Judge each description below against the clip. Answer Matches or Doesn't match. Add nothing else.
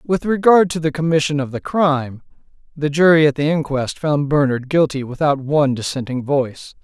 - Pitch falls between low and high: Matches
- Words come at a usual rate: Matches